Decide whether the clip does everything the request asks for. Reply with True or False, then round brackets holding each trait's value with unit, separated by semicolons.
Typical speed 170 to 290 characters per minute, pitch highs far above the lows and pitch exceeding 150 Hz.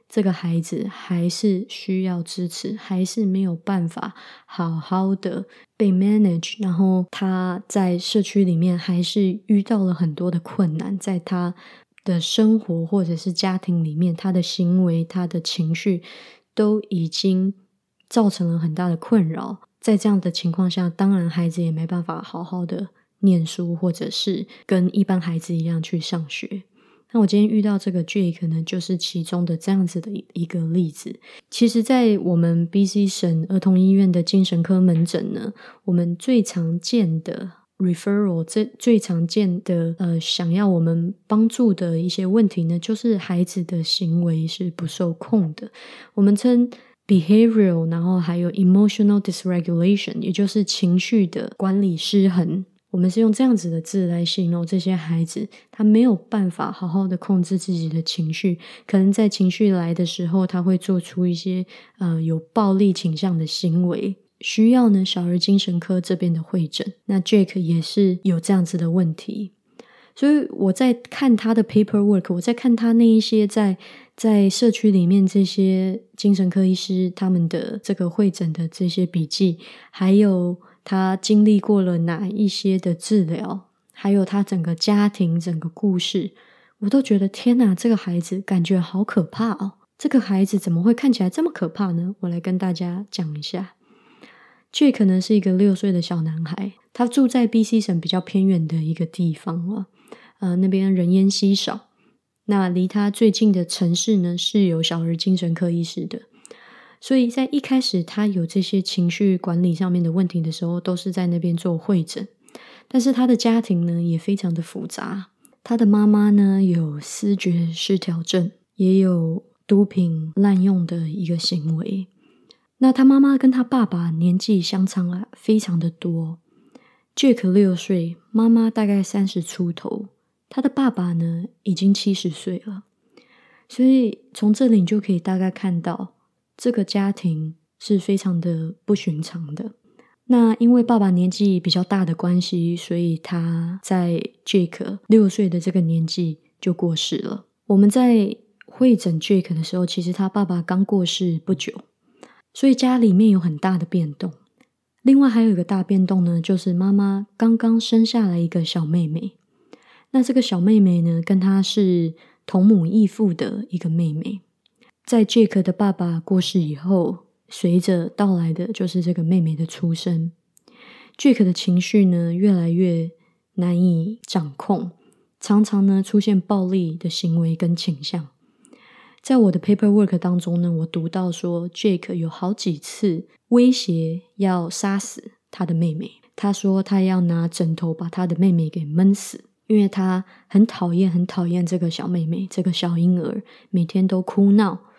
False (260 characters per minute; 3.2 semitones; 190 Hz)